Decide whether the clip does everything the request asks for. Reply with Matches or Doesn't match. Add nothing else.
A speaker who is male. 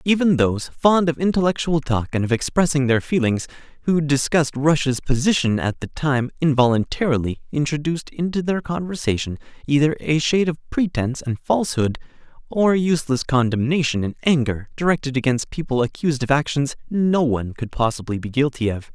Matches